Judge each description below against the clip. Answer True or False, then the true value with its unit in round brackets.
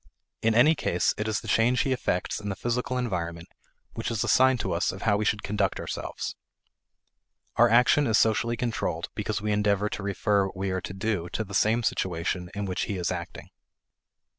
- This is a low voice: True (105 Hz)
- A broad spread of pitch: False (3.7 semitones)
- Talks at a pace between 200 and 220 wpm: True (205 wpm)